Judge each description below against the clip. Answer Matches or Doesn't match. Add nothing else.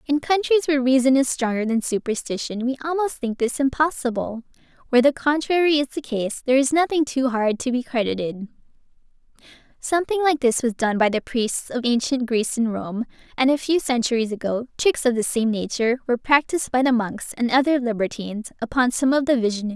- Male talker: Doesn't match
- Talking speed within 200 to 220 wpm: Matches